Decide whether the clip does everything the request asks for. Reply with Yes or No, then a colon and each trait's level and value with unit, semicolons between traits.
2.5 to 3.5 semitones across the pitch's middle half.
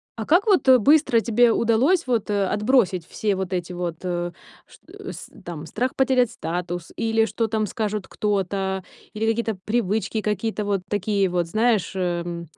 No: average, 3.9 semitones